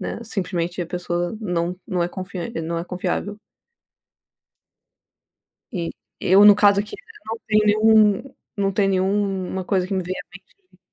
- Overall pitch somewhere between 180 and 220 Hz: Yes, high, 190 Hz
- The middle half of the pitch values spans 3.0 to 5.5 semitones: No, narrow, 2.6 semitones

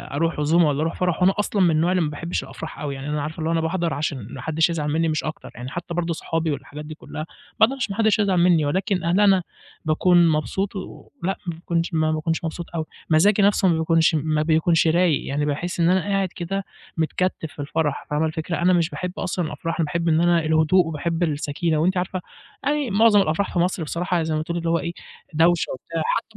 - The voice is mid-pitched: Yes, medium, 165 Hz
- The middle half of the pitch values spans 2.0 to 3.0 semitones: Yes, narrow, 2.6 semitones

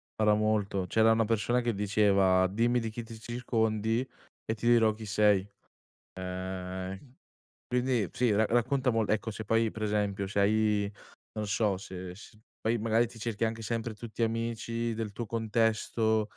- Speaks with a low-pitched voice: Yes, low, 110 Hz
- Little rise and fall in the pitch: Yes, narrow, 2.0 semitones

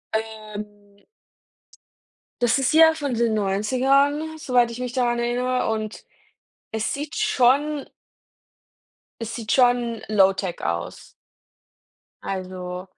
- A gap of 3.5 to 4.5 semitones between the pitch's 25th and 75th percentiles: Yes, average, 4.0 semitones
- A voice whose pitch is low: No, high, 240 Hz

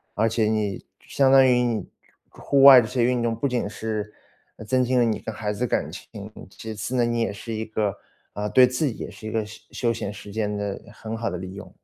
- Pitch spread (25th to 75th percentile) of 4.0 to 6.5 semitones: No, average, 2.9 semitones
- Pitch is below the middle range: Yes, low, 110 Hz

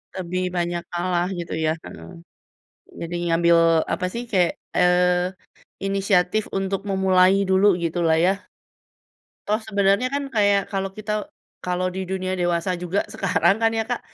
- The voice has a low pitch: No, medium, 185 Hz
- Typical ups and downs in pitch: No, narrow, 2.0 semitones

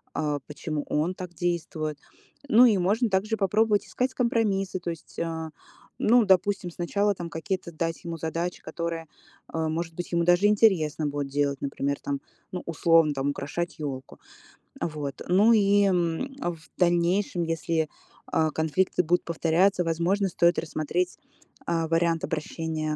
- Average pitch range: Yes, average, 3.1 semitones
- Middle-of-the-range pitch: Yes, medium, 170 Hz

